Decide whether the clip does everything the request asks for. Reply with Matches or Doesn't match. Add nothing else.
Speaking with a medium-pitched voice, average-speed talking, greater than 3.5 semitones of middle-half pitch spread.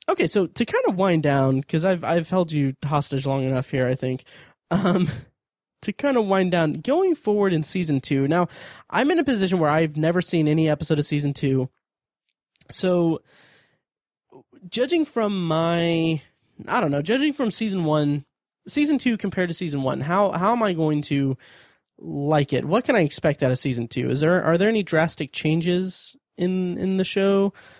Matches